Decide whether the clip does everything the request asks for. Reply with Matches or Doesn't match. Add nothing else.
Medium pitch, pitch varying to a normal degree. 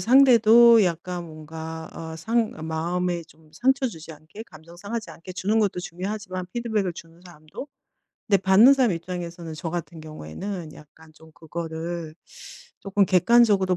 Matches